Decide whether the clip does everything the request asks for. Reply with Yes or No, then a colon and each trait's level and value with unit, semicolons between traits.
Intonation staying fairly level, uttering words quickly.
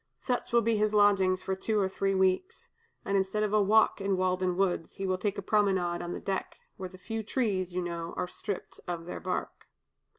Yes: narrow, 2.2 semitones; fast, 210 wpm